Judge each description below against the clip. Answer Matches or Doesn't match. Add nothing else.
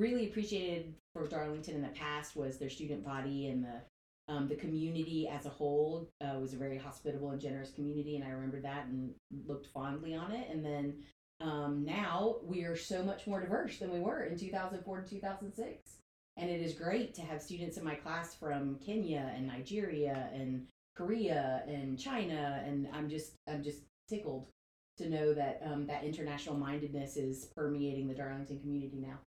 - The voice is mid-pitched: Matches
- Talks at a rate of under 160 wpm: Doesn't match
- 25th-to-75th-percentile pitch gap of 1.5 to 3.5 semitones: Matches